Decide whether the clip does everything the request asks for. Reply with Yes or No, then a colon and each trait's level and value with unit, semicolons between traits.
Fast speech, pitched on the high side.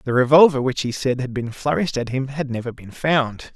No: fast, 235 wpm; low, 130 Hz